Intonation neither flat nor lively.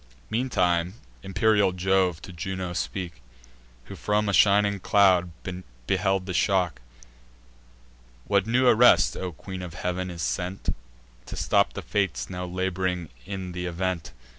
No: narrow, 1.9 semitones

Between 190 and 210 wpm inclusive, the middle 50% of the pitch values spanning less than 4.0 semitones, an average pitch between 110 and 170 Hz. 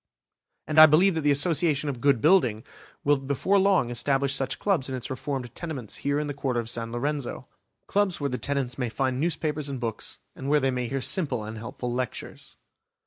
Yes: average, 200 wpm; average, 3.3 semitones; medium, 140 Hz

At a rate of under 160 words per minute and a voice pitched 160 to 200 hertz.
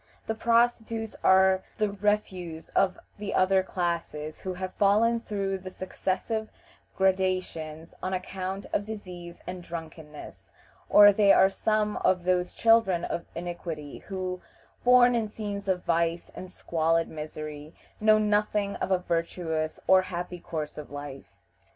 Yes: average, 140 wpm; medium, 185 Hz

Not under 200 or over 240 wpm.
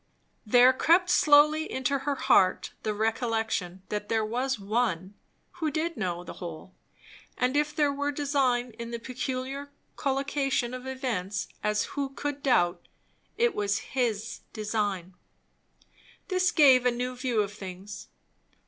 No: average, 140 wpm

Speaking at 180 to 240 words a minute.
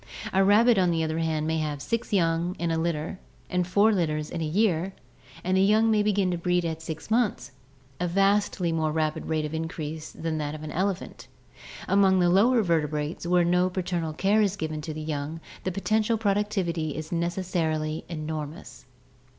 Yes: average, 185 wpm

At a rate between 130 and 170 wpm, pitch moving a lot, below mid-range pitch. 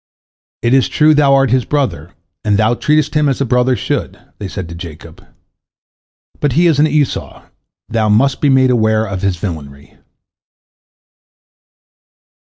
Yes: average, 155 wpm; wide, 5.7 semitones; low, 125 Hz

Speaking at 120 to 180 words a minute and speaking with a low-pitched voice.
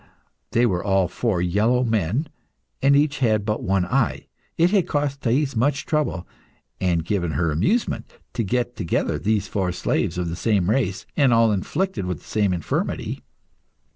Yes: average, 170 wpm; low, 110 Hz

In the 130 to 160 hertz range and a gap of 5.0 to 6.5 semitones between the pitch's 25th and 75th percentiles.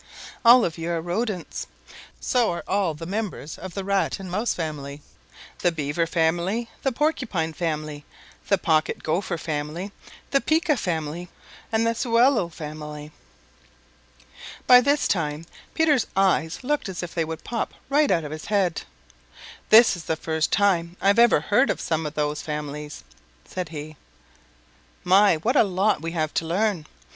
No: medium, 175 Hz; wide, 5.5 semitones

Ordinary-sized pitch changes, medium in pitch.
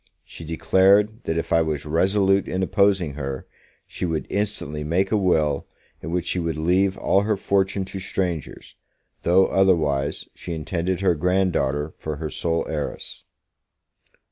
No: average, 3.6 semitones; very low, 90 Hz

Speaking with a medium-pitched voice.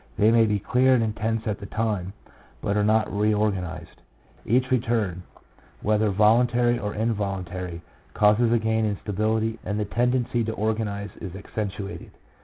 No: low, 110 Hz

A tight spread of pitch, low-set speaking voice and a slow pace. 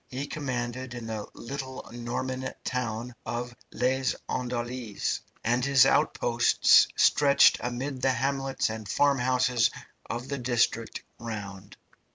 Yes: narrow, 2.0 semitones; low, 125 Hz; slow, 115 wpm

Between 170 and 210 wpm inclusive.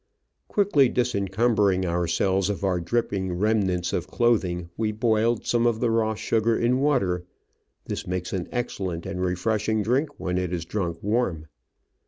No: average, 155 wpm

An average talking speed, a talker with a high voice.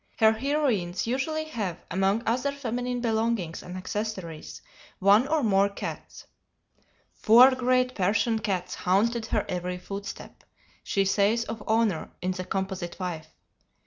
No: slow, 130 wpm; high, 215 Hz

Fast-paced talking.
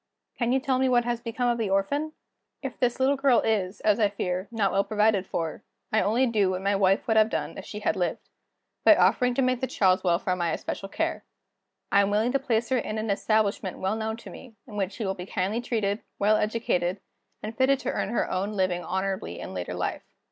Yes: fast, 230 wpm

